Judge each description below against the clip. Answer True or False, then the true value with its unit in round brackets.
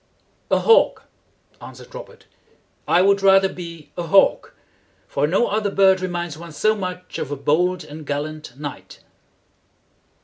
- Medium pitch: True (180 Hz)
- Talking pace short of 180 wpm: True (140 wpm)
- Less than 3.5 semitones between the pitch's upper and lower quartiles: False (4.0 semitones)